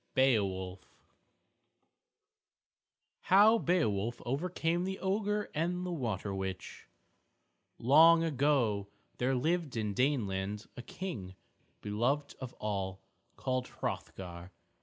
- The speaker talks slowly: Yes, slow, 95 wpm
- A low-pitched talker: Yes, low, 130 Hz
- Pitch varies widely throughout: Yes, wide, 8.6 semitones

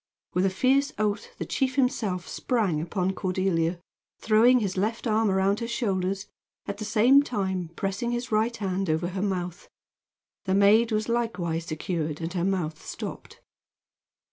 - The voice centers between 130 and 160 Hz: No, high, 195 Hz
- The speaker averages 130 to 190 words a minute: Yes, average, 155 wpm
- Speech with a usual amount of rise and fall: Yes, average, 3.9 semitones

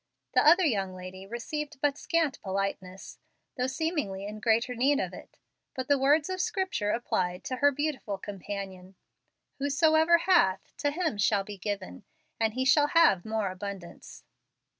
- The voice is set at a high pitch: Yes, high, 235 Hz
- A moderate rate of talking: Yes, average, 155 wpm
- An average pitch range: No, wide, 7.1 semitones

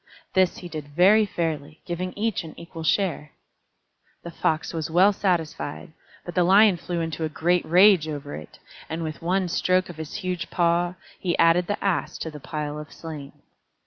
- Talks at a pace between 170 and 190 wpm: Yes, average, 180 wpm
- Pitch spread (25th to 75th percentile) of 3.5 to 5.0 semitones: No, narrow, 2.6 semitones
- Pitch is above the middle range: No, medium, 170 Hz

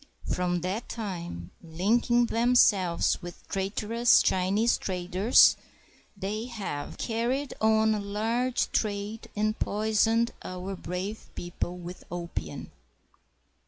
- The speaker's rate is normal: No, slow, 100 wpm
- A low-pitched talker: No, high, 205 Hz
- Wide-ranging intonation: No, average, 3.9 semitones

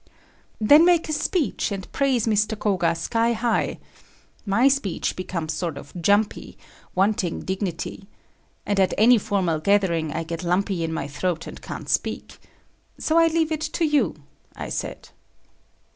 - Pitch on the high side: Yes, high, 200 Hz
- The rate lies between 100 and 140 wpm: No, average, 150 wpm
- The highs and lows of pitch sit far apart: Yes, wide, 6.3 semitones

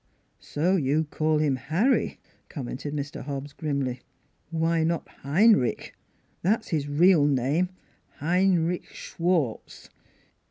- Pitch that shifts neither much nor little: Yes, average, 3.6 semitones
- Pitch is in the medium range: Yes, medium, 155 Hz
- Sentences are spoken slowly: Yes, slow, 110 wpm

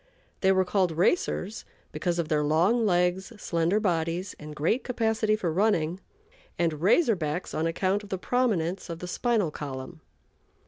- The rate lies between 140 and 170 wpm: Yes, average, 155 wpm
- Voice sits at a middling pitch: Yes, medium, 180 Hz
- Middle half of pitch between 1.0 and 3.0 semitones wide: No, average, 4.3 semitones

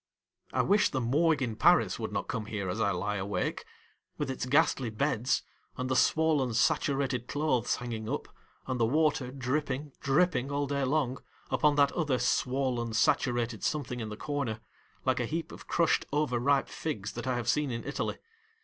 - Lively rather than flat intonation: No, average, 3.7 semitones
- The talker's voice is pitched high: No, low, 130 Hz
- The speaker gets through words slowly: No, average, 180 wpm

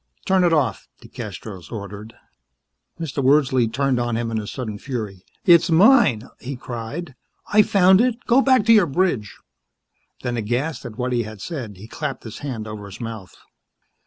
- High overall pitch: No, low, 125 Hz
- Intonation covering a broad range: Yes, wide, 7.2 semitones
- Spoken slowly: No, average, 170 wpm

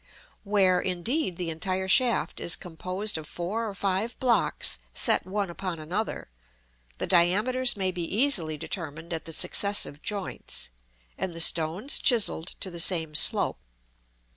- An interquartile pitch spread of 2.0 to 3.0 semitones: No, average, 3.8 semitones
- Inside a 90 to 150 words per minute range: Yes, average, 140 wpm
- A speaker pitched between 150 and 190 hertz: Yes, medium, 185 Hz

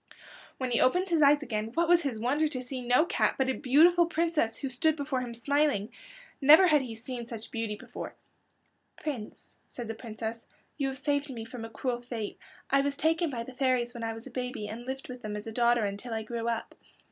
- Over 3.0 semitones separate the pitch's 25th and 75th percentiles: Yes, average, 3.9 semitones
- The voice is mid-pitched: No, very high, 250 Hz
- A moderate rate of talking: No, fast, 225 wpm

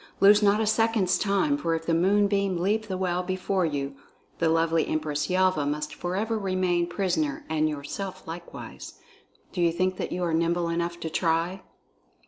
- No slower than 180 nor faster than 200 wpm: No, average, 170 wpm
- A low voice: No, medium, 175 Hz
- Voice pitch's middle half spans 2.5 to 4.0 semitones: Yes, average, 3.1 semitones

